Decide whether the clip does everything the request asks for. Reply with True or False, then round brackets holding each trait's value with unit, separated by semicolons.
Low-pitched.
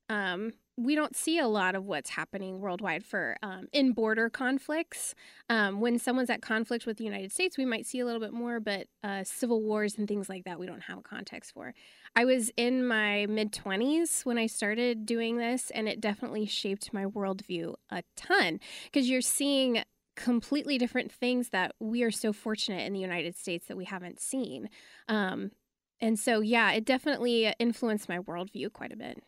False (225 Hz)